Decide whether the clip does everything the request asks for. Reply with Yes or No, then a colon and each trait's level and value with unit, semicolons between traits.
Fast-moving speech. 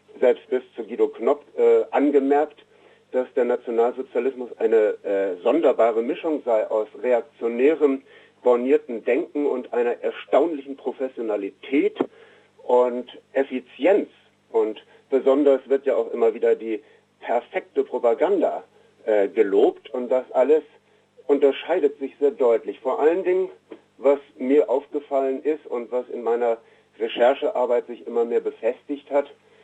No: slow, 125 wpm